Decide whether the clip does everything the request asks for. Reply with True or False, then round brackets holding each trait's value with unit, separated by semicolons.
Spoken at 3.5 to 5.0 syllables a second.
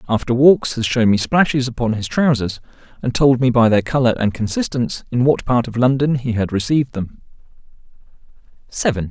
False (5.6 syllables/s)